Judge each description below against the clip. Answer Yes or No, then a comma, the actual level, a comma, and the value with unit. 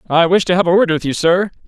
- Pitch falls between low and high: Yes, medium, 175 Hz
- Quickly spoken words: Yes, fast, 325 wpm